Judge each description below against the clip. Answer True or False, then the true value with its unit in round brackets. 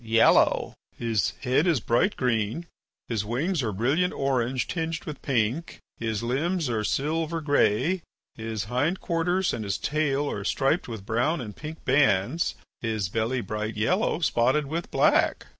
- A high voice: False (130 Hz)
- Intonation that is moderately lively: False (6.2 semitones)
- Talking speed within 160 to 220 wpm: False (150 wpm)